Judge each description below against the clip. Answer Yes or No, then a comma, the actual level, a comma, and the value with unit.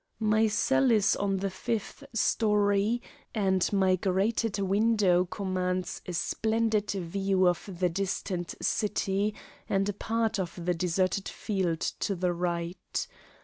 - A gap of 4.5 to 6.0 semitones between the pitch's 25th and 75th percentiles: No, narrow, 2.5 semitones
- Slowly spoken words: Yes, slow, 130 wpm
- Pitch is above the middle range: Yes, high, 195 Hz